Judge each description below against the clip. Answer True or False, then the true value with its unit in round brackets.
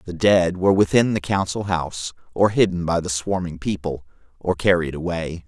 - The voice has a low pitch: True (90 Hz)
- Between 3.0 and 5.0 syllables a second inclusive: False (5.2 syllables/s)